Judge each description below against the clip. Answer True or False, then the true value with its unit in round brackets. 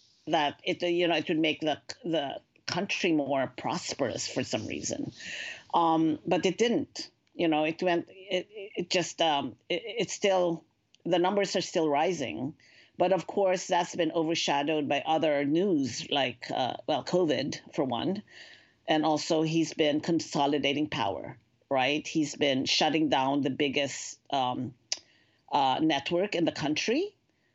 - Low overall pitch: False (160 Hz)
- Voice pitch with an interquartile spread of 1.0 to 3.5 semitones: True (3.1 semitones)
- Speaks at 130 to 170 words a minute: True (150 wpm)